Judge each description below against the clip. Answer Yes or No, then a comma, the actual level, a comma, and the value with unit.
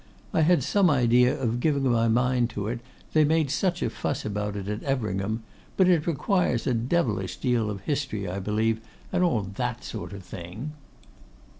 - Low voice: Yes, low, 120 Hz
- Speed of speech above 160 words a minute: Yes, average, 180 wpm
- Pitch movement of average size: No, wide, 5.9 semitones